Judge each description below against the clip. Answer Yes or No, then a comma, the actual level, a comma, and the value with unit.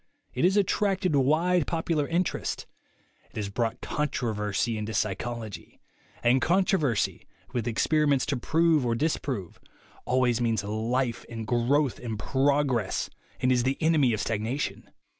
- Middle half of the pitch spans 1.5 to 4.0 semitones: No, average, 5.1 semitones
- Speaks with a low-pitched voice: Yes, low, 130 Hz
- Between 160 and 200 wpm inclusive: No, slow, 135 wpm